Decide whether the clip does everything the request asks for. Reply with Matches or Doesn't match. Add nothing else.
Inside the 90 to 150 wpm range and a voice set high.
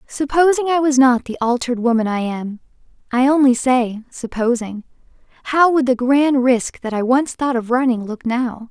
Doesn't match